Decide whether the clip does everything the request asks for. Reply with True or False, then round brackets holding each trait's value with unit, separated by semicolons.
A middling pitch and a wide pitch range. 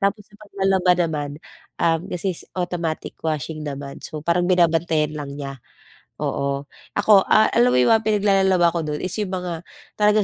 False (175 Hz; 4.2 semitones)